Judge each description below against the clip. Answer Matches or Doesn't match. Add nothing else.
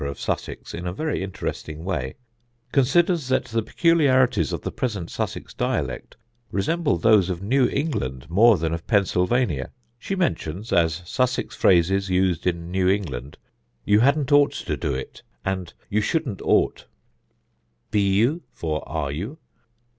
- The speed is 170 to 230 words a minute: Doesn't match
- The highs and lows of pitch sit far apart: Matches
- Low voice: Matches